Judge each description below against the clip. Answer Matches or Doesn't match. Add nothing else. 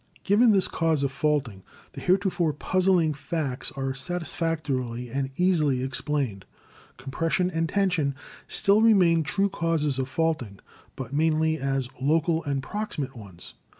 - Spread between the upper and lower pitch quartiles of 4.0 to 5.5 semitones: Matches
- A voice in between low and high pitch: Matches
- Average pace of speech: Doesn't match